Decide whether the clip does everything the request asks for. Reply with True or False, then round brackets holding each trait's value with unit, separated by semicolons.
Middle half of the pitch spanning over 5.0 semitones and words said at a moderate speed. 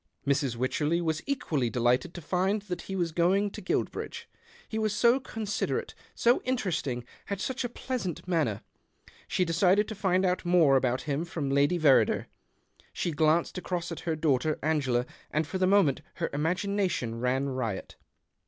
True (5.5 semitones; 160 wpm)